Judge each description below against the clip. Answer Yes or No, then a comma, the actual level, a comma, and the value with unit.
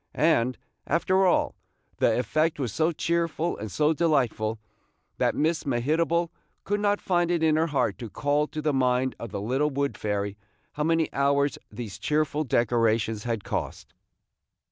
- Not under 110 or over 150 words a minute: No, average, 160 wpm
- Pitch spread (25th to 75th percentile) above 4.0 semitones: Yes, wide, 5.5 semitones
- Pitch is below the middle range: No, medium, 145 Hz